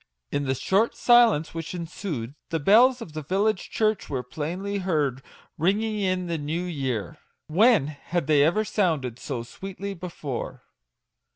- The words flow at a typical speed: Yes, average, 155 wpm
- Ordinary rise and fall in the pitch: No, wide, 5.7 semitones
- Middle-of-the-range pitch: Yes, medium, 170 Hz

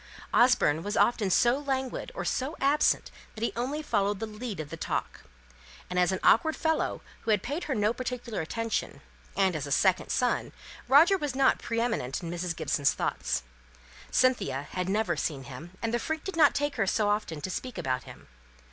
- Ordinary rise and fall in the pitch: No, wide, 6.7 semitones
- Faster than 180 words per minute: Yes, average, 190 wpm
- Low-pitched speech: No, high, 220 Hz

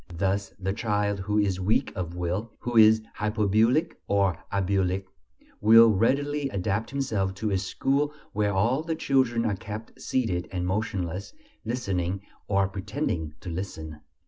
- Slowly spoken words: No, average, 145 wpm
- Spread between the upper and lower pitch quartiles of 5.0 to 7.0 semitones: No, average, 3.2 semitones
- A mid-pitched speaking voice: No, low, 100 Hz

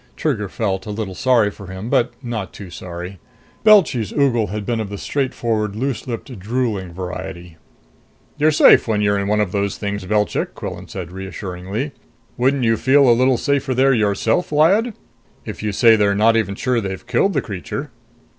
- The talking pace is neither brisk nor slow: Yes, average, 180 wpm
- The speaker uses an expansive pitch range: No, average, 4.5 semitones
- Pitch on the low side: Yes, low, 110 Hz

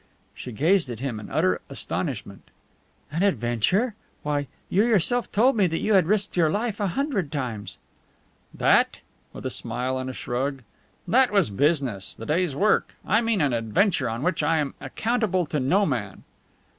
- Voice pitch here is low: No, medium, 160 Hz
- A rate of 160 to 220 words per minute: Yes, average, 170 wpm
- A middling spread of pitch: No, wide, 7.9 semitones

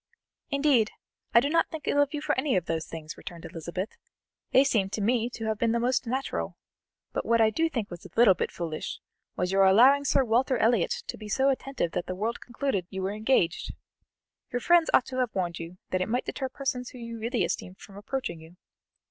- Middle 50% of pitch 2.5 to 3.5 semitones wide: No, wide, 5.6 semitones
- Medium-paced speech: No, fast, 215 wpm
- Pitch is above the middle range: Yes, high, 230 Hz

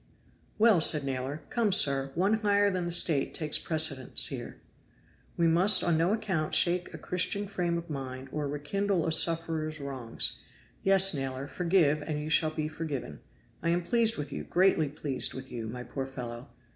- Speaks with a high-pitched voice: No, medium, 155 Hz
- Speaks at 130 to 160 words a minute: No, average, 175 wpm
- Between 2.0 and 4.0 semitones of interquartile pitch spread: No, average, 4.5 semitones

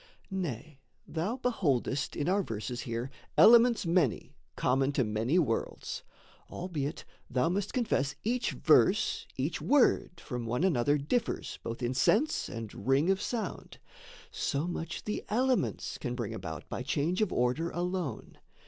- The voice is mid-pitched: Yes, medium, 155 Hz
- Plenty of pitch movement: Yes, wide, 7.7 semitones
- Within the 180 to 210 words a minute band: No, average, 140 wpm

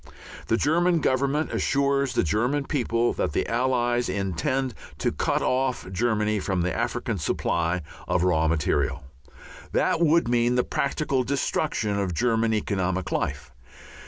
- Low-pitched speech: Yes, low, 120 Hz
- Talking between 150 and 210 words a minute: No, slow, 135 wpm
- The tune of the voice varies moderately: No, wide, 6.4 semitones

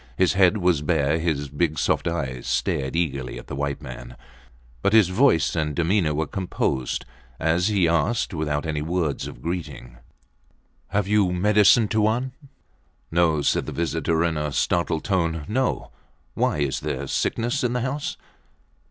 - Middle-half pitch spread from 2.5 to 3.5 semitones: No, average, 4.9 semitones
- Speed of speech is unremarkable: Yes, average, 155 wpm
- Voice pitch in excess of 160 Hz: No, very low, 85 Hz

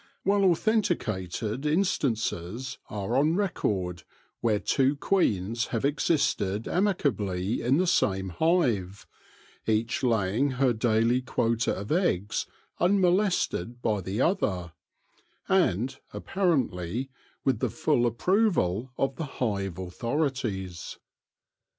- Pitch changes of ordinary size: No, wide, 7.9 semitones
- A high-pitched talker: No, low, 120 Hz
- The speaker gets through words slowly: Yes, slow, 105 wpm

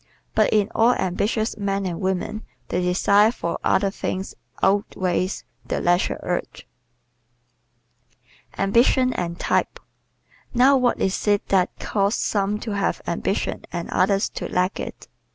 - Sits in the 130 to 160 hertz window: No, high, 195 Hz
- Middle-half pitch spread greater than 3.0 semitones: No, narrow, 2.5 semitones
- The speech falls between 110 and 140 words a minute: Yes, slow, 135 wpm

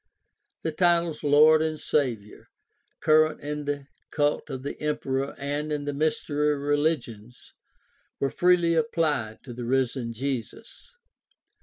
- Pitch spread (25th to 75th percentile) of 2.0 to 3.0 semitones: Yes, average, 2.7 semitones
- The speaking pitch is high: No, medium, 145 Hz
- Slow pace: Yes, slow, 125 wpm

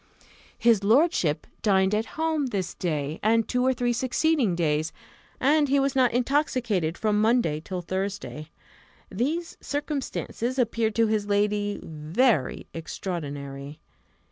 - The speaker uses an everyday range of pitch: No, wide, 6.7 semitones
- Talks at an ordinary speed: No, slow, 125 wpm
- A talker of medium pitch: No, high, 215 Hz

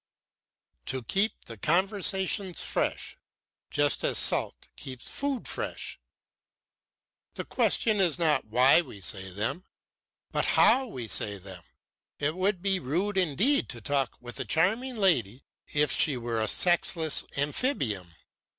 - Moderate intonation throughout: No, wide, 8.4 semitones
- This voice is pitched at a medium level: Yes, medium, 155 Hz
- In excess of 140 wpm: No, slow, 135 wpm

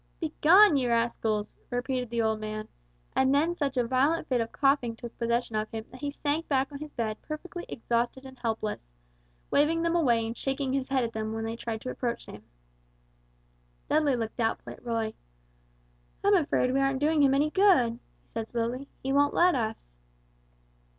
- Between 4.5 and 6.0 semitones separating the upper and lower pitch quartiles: No, average, 3.9 semitones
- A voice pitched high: Yes, very high, 255 Hz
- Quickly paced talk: No, average, 185 wpm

